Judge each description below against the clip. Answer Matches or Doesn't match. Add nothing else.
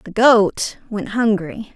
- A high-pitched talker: Matches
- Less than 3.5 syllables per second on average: Matches